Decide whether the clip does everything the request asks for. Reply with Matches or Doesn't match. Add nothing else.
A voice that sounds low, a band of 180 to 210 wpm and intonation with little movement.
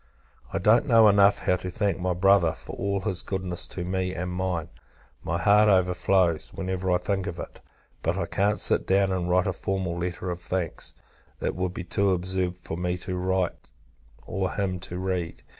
Matches